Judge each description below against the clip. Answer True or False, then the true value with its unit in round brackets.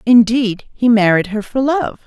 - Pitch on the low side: False (230 Hz)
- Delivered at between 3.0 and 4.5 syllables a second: True (4.3 syllables/s)